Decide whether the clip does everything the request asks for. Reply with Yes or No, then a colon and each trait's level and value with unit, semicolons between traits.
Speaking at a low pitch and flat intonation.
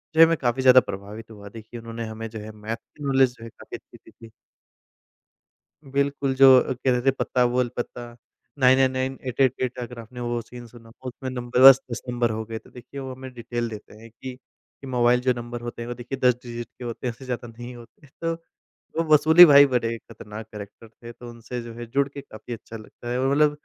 Yes: low, 120 Hz; narrow, 2.2 semitones